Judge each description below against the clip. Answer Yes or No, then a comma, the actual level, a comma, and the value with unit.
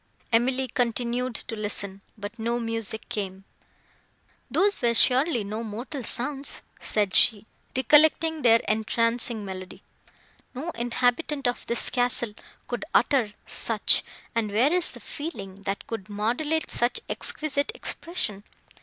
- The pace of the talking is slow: Yes, slow, 125 wpm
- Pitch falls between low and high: No, high, 235 Hz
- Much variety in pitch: No, average, 3.8 semitones